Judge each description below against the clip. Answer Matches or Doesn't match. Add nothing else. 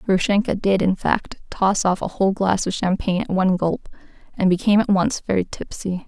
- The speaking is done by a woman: Matches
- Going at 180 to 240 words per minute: Matches